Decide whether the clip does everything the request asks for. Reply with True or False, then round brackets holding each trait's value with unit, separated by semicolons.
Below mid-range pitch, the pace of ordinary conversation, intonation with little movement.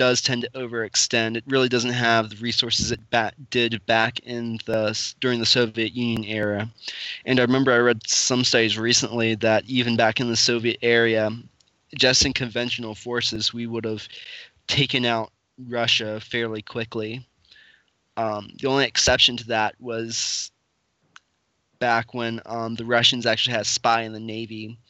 True (115 Hz; 160 wpm; 1.6 semitones)